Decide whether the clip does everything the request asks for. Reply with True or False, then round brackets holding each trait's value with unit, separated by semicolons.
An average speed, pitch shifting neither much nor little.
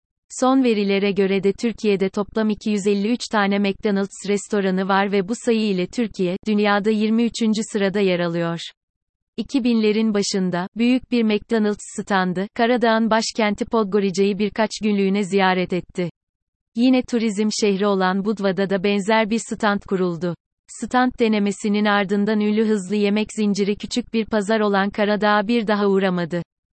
False (130 wpm; 2.2 semitones)